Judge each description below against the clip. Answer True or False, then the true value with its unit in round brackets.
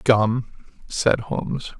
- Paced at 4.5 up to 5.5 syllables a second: False (3.1 syllables/s)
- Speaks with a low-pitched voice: True (120 Hz)